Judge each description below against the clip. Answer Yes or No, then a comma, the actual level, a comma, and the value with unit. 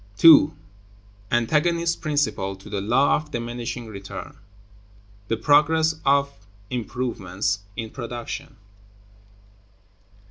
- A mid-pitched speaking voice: No, low, 120 Hz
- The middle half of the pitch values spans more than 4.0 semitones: Yes, wide, 5.5 semitones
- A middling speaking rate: No, slow, 95 wpm